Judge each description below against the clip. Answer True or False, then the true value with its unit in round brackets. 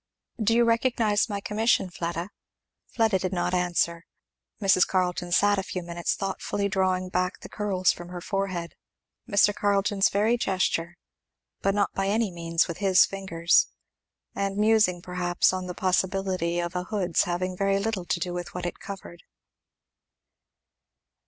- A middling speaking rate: True (150 wpm)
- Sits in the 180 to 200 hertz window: True (185 Hz)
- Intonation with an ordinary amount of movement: False (2.3 semitones)